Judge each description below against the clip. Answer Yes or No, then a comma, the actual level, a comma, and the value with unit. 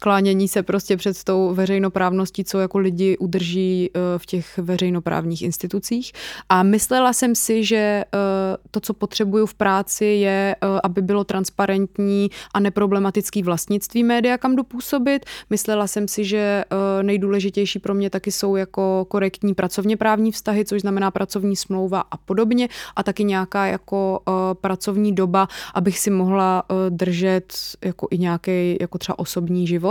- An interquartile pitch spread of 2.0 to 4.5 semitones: No, narrow, 1.5 semitones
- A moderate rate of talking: Yes, average, 140 wpm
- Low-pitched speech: No, high, 195 Hz